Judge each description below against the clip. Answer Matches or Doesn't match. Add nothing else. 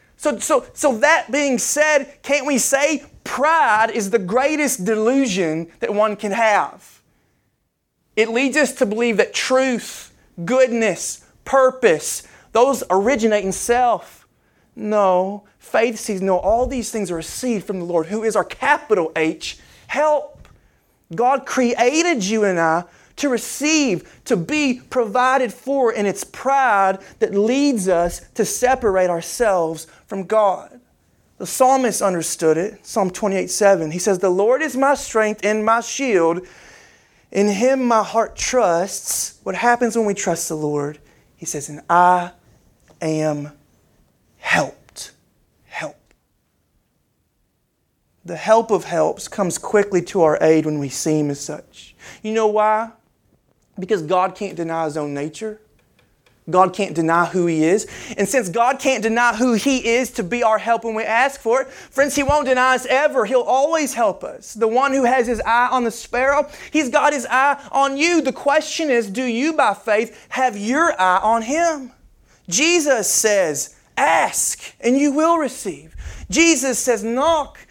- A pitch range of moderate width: Doesn't match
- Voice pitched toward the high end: Matches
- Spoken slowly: Doesn't match